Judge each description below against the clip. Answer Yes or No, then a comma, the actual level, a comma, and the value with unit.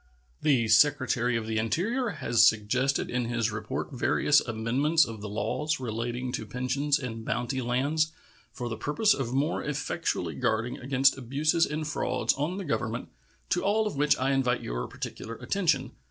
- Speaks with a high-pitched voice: No, low, 130 Hz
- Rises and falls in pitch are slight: No, average, 4.2 semitones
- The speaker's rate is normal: Yes, average, 165 wpm